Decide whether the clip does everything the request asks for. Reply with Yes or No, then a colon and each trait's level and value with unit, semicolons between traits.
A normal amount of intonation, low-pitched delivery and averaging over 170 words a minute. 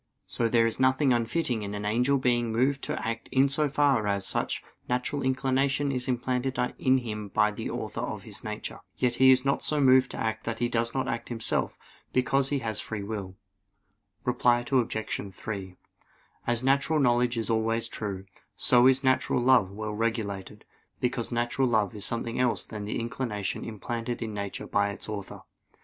Yes: average, 3.1 semitones; low, 120 Hz; average, 180 wpm